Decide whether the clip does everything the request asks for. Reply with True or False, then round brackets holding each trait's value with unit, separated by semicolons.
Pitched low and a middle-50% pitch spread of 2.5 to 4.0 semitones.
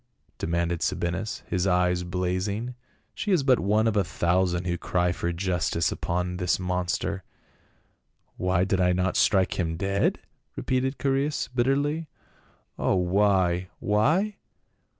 True (95 Hz; 3.4 semitones)